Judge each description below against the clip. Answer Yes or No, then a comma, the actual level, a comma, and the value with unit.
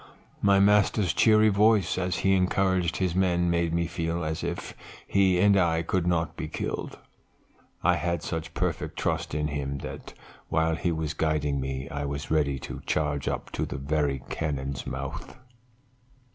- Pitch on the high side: No, very low, 80 Hz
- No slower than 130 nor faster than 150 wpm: No, average, 165 wpm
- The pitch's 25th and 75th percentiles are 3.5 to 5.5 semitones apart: Yes, average, 3.8 semitones